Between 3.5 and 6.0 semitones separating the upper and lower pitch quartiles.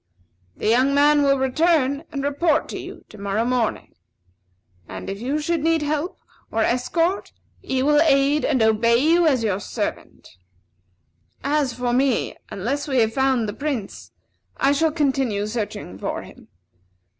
Yes: average, 4.3 semitones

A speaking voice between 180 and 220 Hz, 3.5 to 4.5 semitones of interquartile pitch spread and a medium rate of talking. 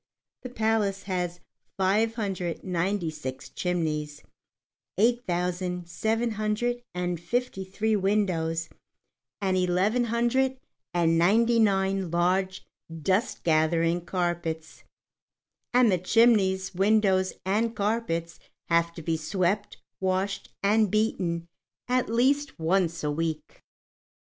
No: high, 190 Hz; average, 4.1 semitones; slow, 110 wpm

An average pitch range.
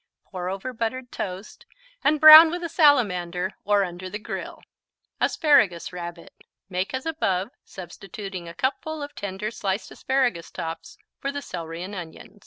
No: wide, 6.6 semitones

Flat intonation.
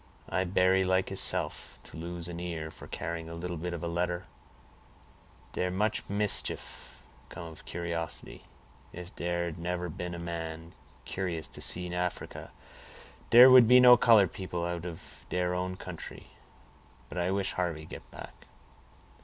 Yes: narrow, 1.6 semitones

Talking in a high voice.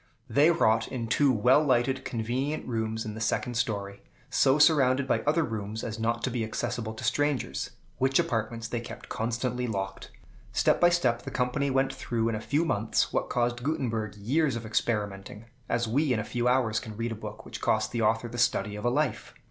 No: low, 120 Hz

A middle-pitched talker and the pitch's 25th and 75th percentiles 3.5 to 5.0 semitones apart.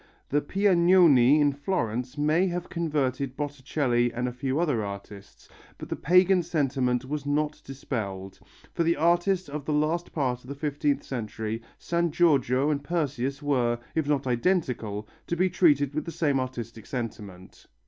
Yes: medium, 145 Hz; average, 4.6 semitones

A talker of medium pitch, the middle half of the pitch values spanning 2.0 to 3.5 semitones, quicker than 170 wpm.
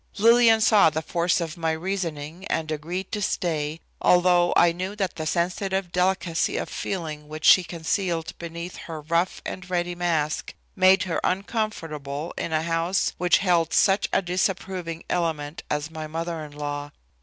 No: medium, 170 Hz; average, 2.8 semitones; average, 160 wpm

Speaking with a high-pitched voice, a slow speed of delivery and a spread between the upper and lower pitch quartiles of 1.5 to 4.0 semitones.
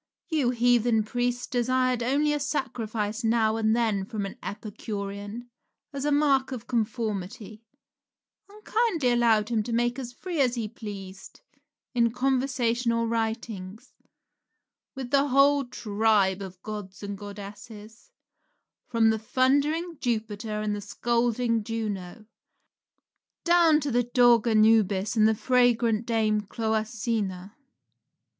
Yes: high, 230 Hz; slow, 125 wpm; average, 2.8 semitones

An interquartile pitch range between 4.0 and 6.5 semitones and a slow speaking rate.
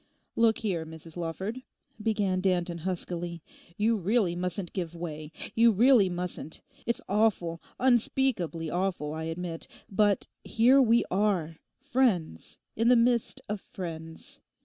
Yes: average, 5.0 semitones; slow, 125 wpm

